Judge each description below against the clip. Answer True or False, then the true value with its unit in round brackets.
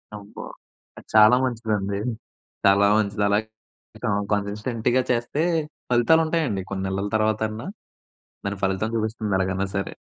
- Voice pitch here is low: True (105 Hz)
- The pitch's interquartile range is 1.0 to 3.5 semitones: True (2.6 semitones)